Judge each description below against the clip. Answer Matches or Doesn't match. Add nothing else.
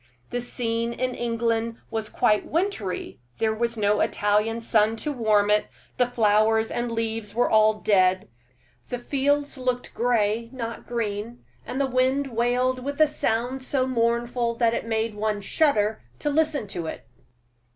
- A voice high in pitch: Matches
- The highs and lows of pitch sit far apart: Doesn't match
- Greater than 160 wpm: Doesn't match